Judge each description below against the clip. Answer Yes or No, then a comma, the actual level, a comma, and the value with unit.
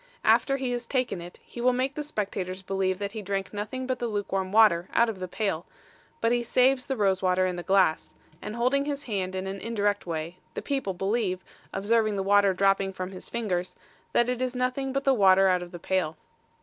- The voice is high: Yes, high, 200 Hz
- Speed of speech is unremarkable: No, fast, 225 wpm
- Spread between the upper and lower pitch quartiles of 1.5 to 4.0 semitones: No, average, 4.5 semitones